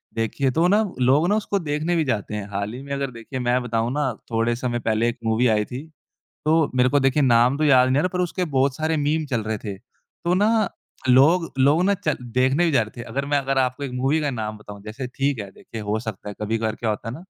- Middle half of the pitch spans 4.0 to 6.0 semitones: Yes, average, 4.6 semitones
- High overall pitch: No, low, 130 Hz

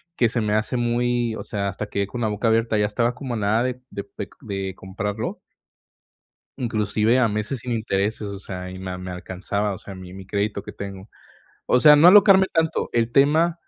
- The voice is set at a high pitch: No, low, 110 Hz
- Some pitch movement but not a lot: Yes, average, 3.4 semitones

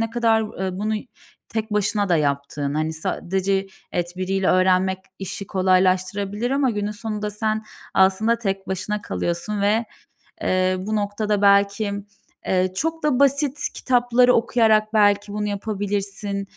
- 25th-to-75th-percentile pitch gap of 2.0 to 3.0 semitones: Yes, narrow, 2.5 semitones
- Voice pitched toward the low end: No, high, 205 Hz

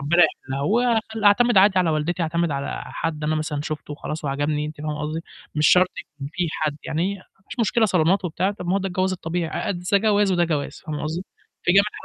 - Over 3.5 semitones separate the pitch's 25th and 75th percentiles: Yes, average, 4.1 semitones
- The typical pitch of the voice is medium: Yes, medium, 170 Hz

